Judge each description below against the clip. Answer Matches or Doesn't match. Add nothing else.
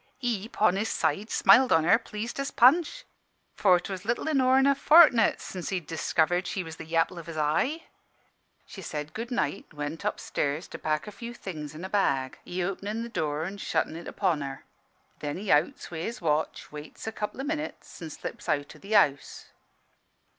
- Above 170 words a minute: Matches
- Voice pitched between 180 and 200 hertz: Matches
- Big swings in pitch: Matches